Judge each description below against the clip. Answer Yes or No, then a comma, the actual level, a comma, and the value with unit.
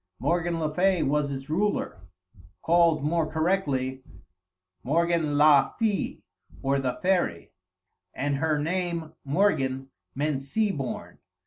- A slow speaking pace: Yes, slow, 115 wpm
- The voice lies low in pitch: No, medium, 155 Hz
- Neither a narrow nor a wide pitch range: Yes, average, 3.9 semitones